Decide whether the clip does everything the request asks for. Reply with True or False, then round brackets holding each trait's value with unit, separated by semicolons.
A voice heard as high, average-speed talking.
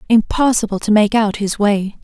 True (215 Hz; 175 wpm)